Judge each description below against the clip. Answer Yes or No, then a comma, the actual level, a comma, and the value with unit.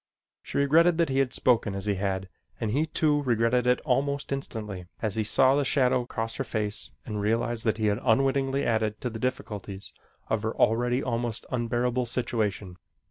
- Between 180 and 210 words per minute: Yes, average, 185 wpm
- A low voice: Yes, low, 120 Hz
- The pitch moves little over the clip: No, average, 3.7 semitones